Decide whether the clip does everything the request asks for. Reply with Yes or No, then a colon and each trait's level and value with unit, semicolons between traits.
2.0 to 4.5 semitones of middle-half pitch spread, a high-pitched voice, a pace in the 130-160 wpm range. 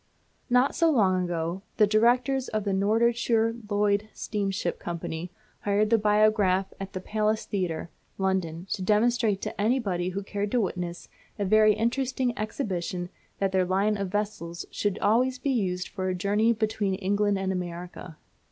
Yes: average, 2.8 semitones; high, 205 Hz; average, 155 wpm